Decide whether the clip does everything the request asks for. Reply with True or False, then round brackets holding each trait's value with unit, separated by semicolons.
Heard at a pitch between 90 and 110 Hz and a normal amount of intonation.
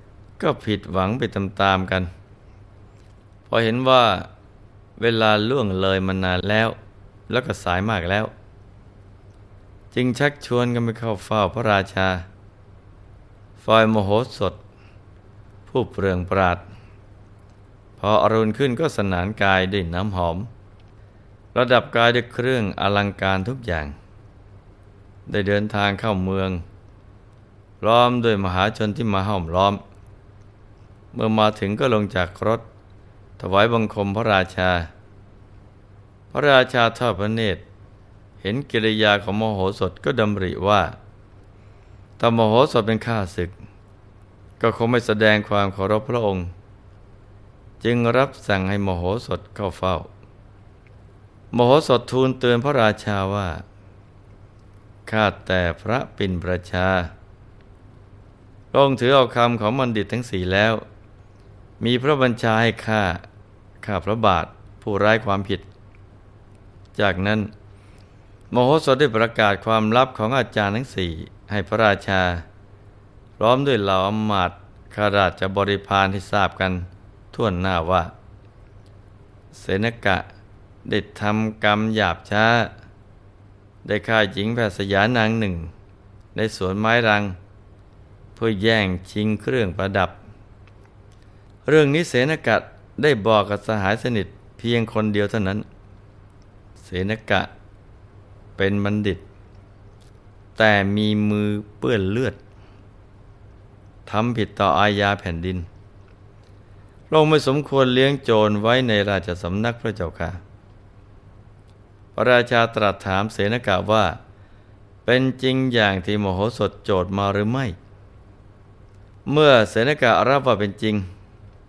False (100 Hz; 1.5 semitones)